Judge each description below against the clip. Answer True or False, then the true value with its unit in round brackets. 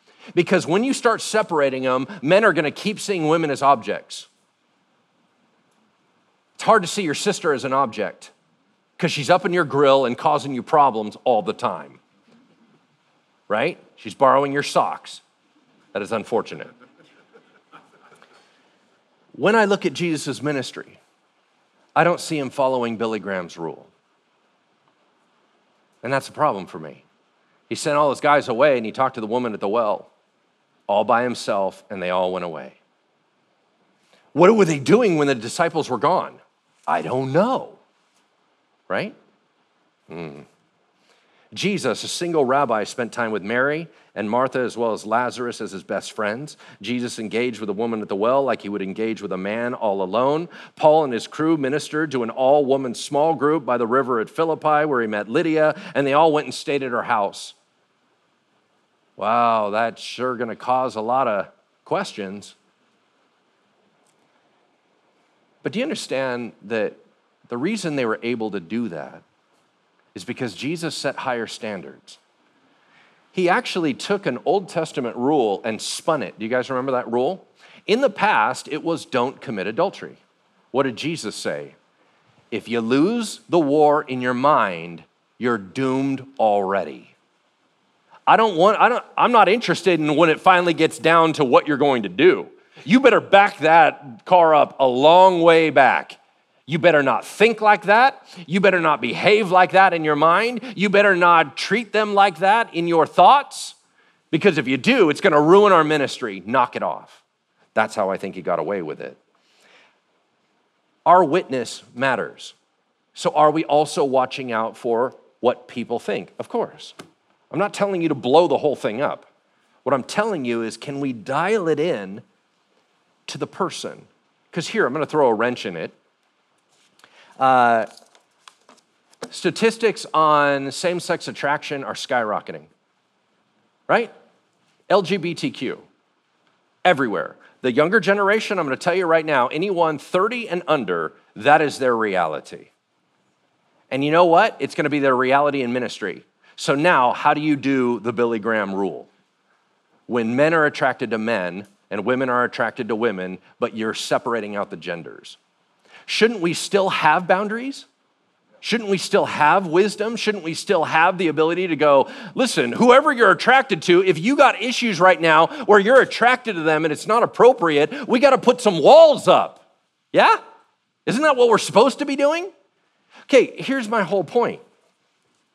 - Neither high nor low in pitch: True (150 Hz)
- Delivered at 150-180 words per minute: True (165 wpm)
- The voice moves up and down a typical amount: False (7.2 semitones)